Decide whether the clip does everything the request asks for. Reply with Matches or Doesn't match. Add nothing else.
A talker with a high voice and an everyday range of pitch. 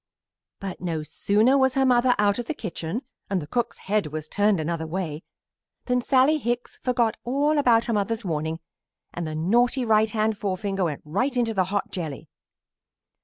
Doesn't match